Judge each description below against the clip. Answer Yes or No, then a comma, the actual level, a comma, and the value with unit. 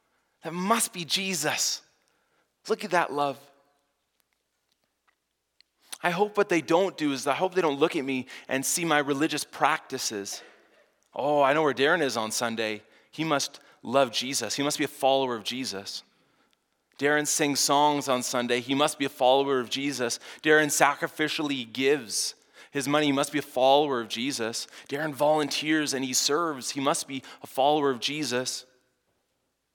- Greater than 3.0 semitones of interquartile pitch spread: No, narrow, 2.6 semitones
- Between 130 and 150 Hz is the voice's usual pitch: Yes, medium, 140 Hz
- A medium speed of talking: Yes, average, 165 wpm